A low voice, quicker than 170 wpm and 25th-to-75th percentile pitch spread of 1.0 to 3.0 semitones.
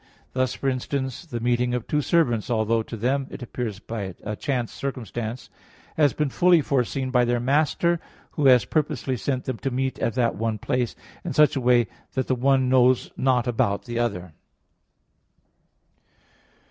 No: low, 125 Hz; average, 165 wpm; narrow, 2.4 semitones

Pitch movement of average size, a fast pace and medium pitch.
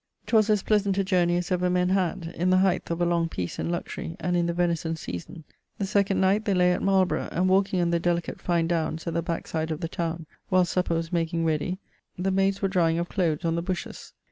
No: narrow, 2.1 semitones; fast, 240 wpm; medium, 175 Hz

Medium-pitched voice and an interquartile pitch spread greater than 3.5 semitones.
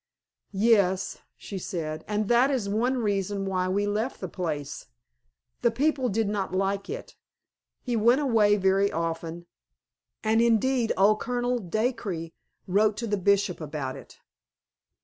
No: high, 205 Hz; average, 3.9 semitones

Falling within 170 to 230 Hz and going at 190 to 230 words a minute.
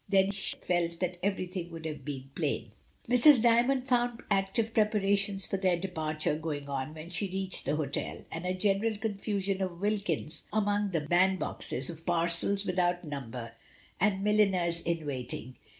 No: medium, 185 Hz; average, 160 wpm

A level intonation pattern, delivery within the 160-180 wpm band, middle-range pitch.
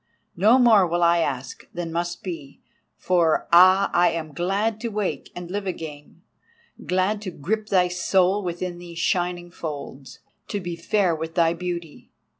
No: narrow, 2.3 semitones; average, 150 wpm; medium, 175 Hz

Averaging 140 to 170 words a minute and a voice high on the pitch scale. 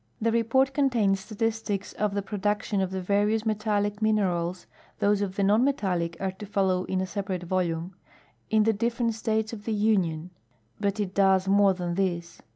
No: average, 180 wpm; high, 200 Hz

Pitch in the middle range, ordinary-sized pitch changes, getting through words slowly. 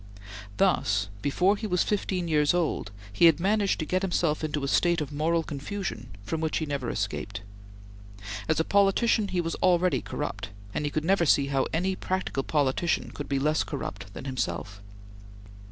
No: medium, 160 Hz; average, 4.8 semitones; average, 175 wpm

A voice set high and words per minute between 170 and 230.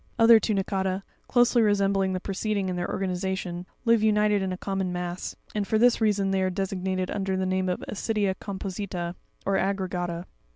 Yes: high, 195 Hz; average, 175 wpm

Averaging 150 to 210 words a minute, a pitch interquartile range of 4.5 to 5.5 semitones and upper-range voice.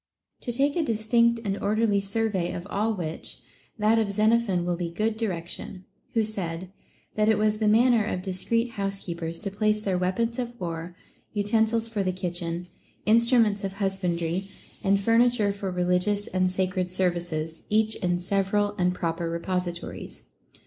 No: average, 160 wpm; average, 3.4 semitones; high, 200 Hz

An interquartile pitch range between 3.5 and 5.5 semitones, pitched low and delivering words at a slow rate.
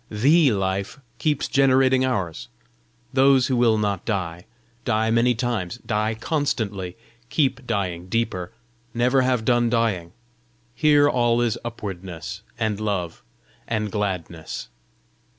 Yes: average, 4.6 semitones; low, 115 Hz; slow, 115 wpm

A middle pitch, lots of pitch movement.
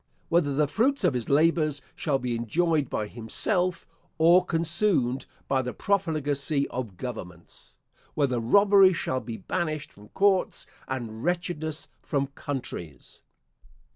Yes: medium, 145 Hz; wide, 5.7 semitones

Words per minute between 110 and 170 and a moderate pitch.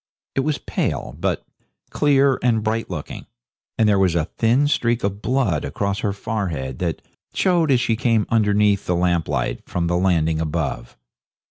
No: average, 165 wpm; low, 105 Hz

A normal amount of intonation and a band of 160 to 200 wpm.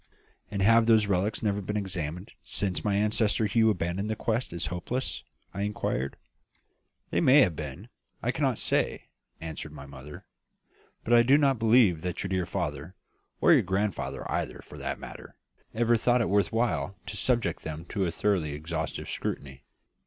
Yes: average, 5.0 semitones; average, 170 wpm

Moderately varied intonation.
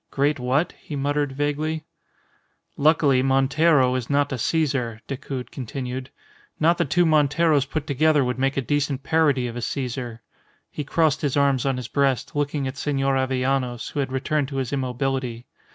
No: narrow, 2.2 semitones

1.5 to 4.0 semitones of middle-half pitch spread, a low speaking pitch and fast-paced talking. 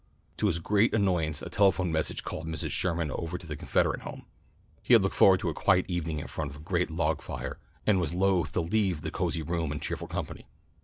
Yes: average, 3.2 semitones; very low, 85 Hz; fast, 225 wpm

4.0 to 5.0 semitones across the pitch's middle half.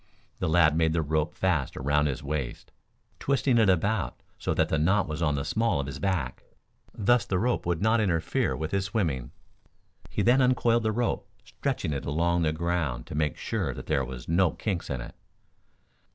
No: wide, 5.5 semitones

